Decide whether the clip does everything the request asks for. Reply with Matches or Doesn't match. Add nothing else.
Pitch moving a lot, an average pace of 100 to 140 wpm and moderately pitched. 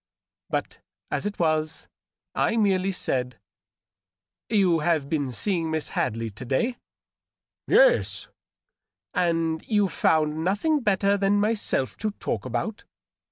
Matches